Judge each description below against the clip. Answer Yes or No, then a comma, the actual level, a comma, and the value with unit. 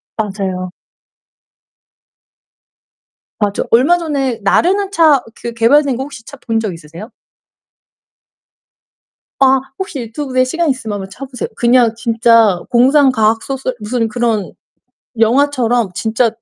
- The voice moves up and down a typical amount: Yes, average, 3.5 semitones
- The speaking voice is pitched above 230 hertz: Yes, high, 240 Hz